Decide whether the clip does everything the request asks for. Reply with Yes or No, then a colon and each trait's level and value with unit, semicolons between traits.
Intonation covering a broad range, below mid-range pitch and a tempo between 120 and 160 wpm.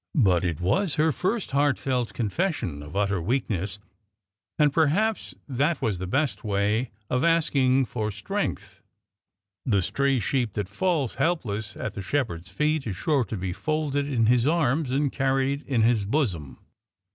Yes: wide, 6.2 semitones; low, 130 Hz; average, 155 wpm